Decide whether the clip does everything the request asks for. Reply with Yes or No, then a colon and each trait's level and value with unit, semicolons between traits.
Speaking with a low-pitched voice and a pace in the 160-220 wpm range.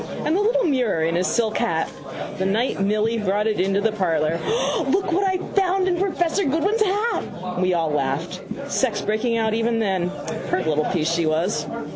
No: high, 215 Hz; average, 190 wpm